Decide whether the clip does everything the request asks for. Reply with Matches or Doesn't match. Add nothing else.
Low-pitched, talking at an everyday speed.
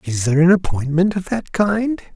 Doesn't match